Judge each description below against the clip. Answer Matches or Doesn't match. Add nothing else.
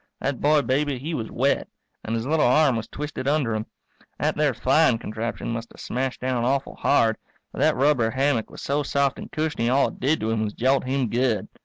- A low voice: Matches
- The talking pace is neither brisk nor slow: Doesn't match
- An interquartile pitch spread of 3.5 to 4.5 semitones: Matches